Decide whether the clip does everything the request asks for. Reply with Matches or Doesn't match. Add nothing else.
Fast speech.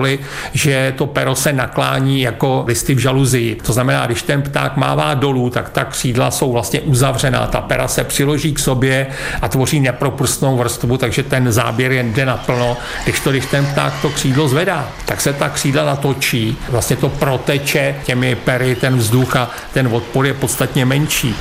Matches